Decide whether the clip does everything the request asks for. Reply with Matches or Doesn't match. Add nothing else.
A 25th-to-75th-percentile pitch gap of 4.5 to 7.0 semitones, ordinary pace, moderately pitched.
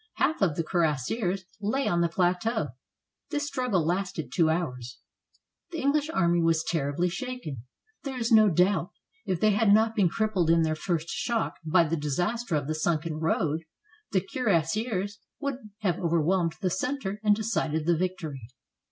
Matches